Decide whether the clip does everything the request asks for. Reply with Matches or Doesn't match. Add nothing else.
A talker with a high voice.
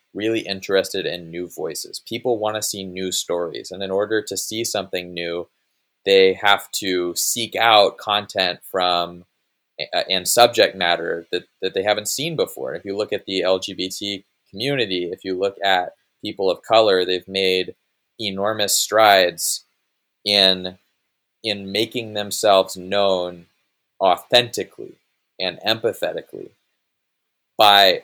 Doesn't match